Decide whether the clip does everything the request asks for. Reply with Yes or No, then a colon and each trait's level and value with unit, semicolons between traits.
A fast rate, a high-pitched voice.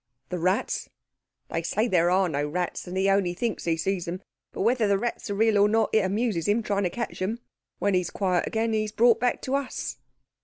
Yes: fast, 235 wpm; high, 200 Hz